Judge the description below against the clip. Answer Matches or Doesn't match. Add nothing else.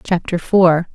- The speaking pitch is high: Doesn't match